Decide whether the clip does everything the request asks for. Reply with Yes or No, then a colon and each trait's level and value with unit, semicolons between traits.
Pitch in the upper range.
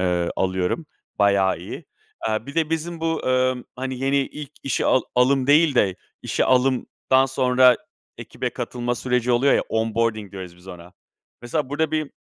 No: low, 125 Hz